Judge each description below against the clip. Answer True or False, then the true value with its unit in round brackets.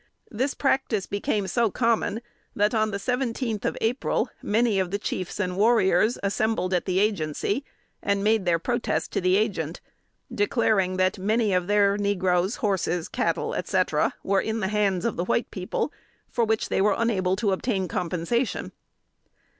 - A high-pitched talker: True (205 Hz)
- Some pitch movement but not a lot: True (3.1 semitones)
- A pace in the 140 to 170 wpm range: True (160 wpm)